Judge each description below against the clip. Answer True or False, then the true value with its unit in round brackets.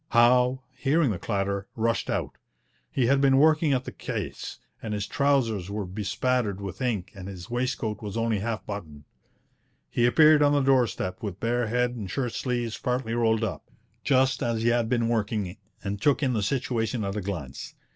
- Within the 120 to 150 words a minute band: False (185 wpm)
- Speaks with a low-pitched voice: True (115 Hz)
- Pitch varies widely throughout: False (3.8 semitones)